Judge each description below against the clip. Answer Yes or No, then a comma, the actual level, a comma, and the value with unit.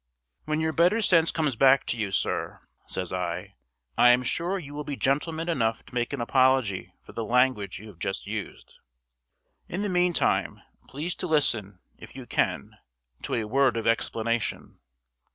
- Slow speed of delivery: No, average, 170 wpm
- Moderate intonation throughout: No, wide, 6.0 semitones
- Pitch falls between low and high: No, low, 130 Hz